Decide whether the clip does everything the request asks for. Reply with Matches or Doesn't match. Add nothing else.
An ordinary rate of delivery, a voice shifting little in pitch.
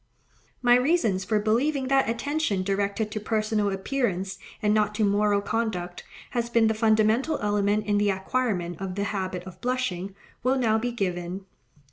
Doesn't match